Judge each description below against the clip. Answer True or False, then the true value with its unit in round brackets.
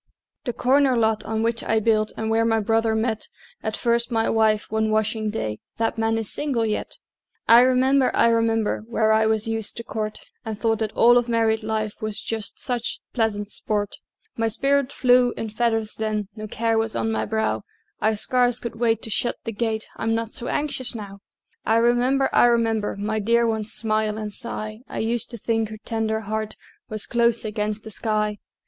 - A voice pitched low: False (225 Hz)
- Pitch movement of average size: False (1.3 semitones)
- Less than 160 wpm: False (195 wpm)